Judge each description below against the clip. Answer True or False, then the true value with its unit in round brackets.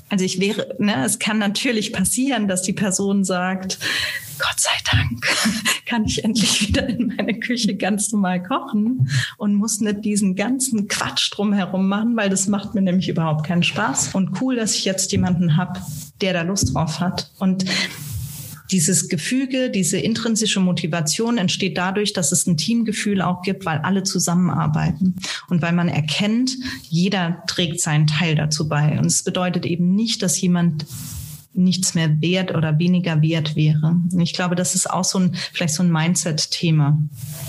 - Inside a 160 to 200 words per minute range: True (170 wpm)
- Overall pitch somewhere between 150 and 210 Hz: True (185 Hz)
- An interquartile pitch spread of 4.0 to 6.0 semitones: False (3.5 semitones)